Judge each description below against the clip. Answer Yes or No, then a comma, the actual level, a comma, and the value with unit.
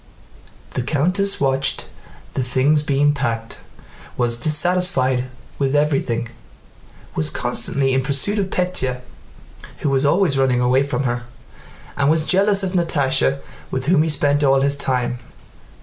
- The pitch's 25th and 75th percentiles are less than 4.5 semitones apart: Yes, average, 3.0 semitones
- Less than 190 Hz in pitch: Yes, medium, 140 Hz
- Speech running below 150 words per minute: Yes, slow, 135 wpm